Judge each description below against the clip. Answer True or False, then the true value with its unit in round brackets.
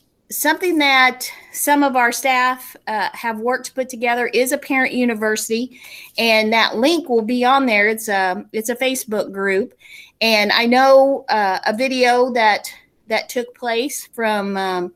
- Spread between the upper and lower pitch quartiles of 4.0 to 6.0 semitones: False (3.0 semitones)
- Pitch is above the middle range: True (245 Hz)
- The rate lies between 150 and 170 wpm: True (165 wpm)